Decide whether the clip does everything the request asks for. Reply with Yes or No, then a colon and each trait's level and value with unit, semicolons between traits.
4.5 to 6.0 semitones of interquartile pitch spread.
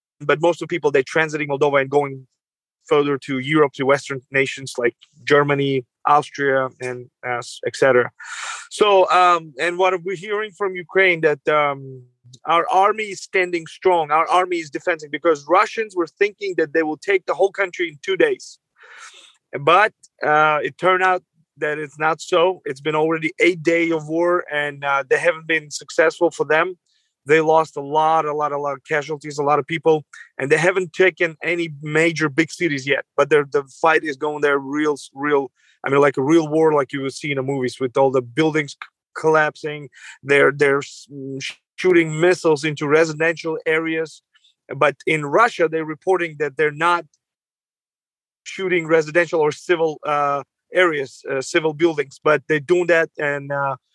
No: average, 3.2 semitones